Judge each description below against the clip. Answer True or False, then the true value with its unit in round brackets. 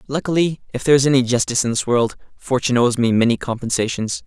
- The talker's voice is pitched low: True (125 Hz)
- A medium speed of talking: True (195 wpm)